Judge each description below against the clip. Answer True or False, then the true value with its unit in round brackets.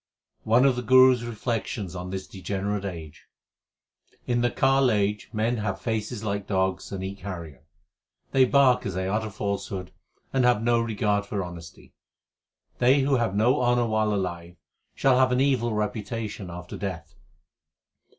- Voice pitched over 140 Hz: False (105 Hz)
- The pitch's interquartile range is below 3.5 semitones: False (4.2 semitones)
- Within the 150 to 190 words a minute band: True (160 wpm)